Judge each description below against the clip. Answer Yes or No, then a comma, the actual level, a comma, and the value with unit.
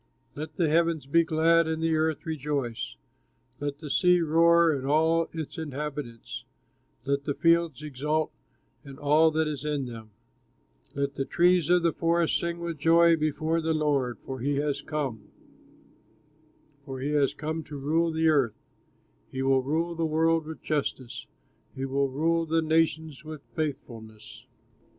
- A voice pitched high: No, medium, 155 Hz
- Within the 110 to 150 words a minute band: No, average, 160 wpm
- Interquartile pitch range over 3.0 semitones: No, average, 2.7 semitones